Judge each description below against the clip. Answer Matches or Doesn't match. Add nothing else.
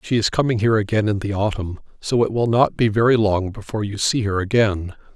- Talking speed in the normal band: Doesn't match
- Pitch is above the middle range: Doesn't match